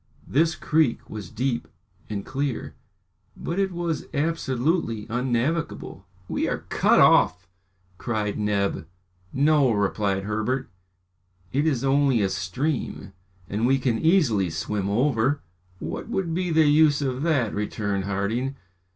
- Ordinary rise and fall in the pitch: No, wide, 6.2 semitones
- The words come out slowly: Yes, slow, 125 wpm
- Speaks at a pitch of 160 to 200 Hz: No, low, 125 Hz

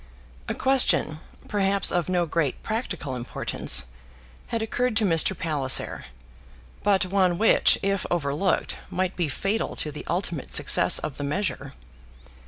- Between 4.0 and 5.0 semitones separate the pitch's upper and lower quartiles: Yes, average, 4.6 semitones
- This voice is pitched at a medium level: Yes, medium, 180 Hz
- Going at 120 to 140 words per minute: Yes, slow, 135 wpm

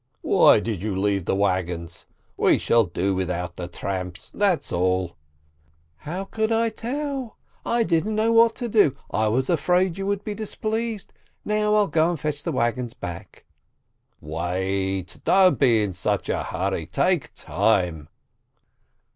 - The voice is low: Yes, low, 115 Hz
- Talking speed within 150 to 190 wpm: Yes, average, 155 wpm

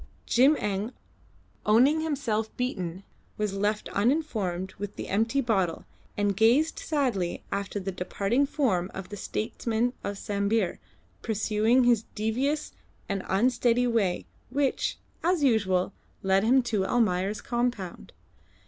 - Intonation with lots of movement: No, average, 4.1 semitones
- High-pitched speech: Yes, high, 220 Hz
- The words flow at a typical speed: No, slow, 120 wpm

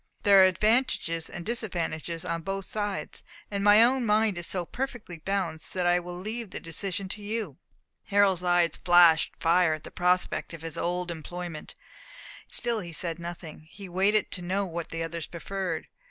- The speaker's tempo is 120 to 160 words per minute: No, average, 175 wpm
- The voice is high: No, medium, 180 Hz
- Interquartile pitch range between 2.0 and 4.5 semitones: Yes, average, 3.2 semitones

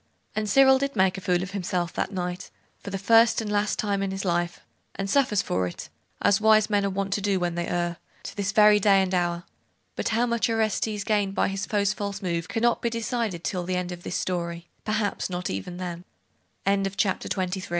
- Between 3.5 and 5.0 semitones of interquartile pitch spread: No, average, 3.1 semitones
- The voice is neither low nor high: No, high, 195 Hz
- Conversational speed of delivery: No, fast, 210 wpm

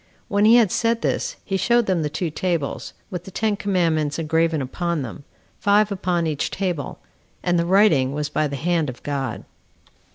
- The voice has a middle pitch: Yes, medium, 170 Hz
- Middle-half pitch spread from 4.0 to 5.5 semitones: Yes, average, 4.7 semitones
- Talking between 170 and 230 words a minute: Yes, average, 185 wpm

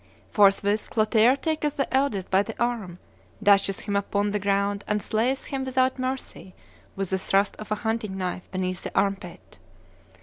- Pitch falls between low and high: No, high, 205 Hz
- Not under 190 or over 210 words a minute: No, average, 170 wpm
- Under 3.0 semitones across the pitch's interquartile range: No, average, 3.6 semitones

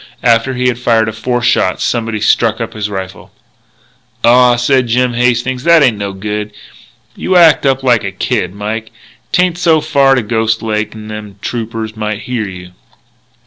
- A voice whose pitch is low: Yes, low, 115 Hz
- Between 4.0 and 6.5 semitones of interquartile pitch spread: No, average, 2.8 semitones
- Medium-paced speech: Yes, average, 170 wpm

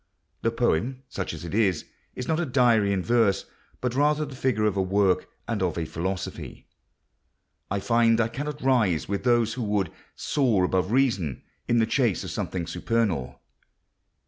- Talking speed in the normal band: Yes, average, 170 wpm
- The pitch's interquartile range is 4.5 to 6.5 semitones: Yes, average, 5.0 semitones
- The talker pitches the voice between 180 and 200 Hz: No, low, 110 Hz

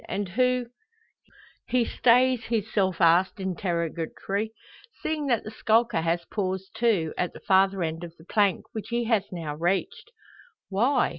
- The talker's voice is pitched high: Yes, high, 195 Hz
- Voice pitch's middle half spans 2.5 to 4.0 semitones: No, average, 4.9 semitones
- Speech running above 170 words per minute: No, average, 155 wpm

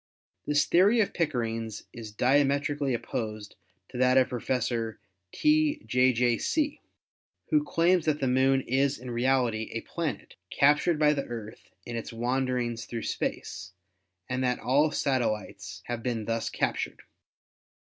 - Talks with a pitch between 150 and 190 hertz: No, low, 125 Hz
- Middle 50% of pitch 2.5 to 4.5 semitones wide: Yes, average, 4.0 semitones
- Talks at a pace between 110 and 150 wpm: Yes, average, 145 wpm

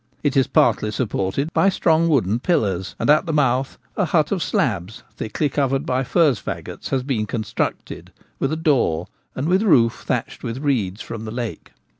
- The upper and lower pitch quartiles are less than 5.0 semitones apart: No, average, 5.3 semitones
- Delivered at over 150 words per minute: Yes, average, 180 wpm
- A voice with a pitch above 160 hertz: No, low, 130 Hz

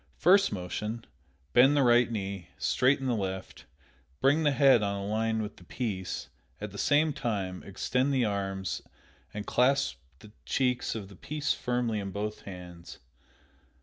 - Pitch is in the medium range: No, low, 110 Hz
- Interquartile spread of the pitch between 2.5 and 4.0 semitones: No, average, 4.7 semitones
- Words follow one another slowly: No, average, 155 wpm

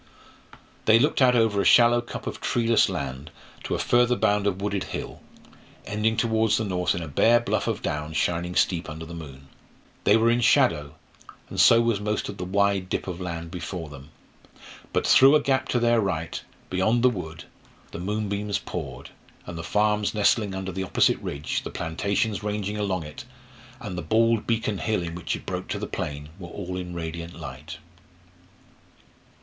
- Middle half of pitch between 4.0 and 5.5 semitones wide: Yes, average, 4.9 semitones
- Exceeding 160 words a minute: Yes, average, 185 wpm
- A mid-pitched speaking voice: No, very low, 95 Hz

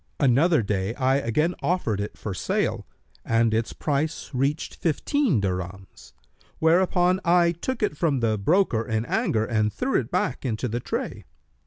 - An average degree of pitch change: No, wide, 7.4 semitones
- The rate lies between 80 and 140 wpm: No, average, 155 wpm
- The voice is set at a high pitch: No, low, 130 Hz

